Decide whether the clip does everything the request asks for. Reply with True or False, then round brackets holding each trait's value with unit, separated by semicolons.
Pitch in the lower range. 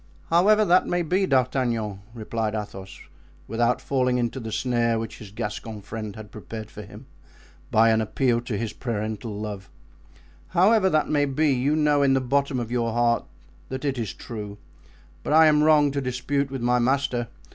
True (120 Hz)